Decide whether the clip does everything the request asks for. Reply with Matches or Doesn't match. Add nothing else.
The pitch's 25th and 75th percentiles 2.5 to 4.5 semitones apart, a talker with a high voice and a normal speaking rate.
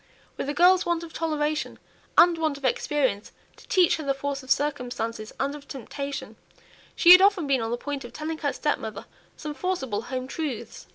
Matches